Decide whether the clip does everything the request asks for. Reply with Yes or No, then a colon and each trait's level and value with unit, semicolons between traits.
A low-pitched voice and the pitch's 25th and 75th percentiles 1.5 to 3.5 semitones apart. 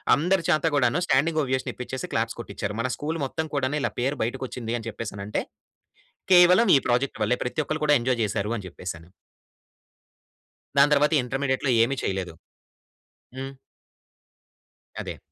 No: low, 130 Hz; average, 4.2 semitones